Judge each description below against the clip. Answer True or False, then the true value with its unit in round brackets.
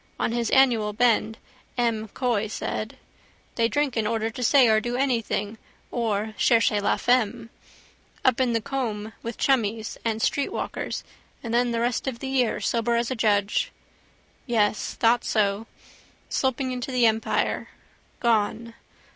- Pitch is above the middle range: True (230 Hz)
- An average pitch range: False (2.1 semitones)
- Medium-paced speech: True (145 wpm)